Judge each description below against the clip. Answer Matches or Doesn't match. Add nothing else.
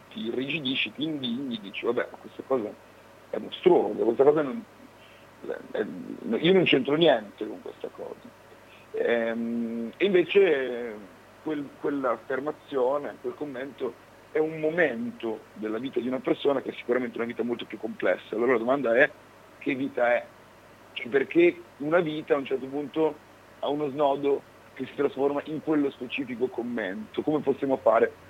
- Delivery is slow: Doesn't match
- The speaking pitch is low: Doesn't match